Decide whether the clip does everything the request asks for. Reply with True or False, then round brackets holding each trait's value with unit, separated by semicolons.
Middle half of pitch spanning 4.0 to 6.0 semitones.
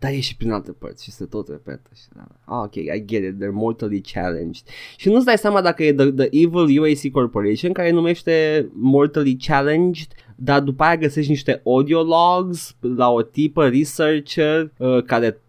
True (5.6 semitones)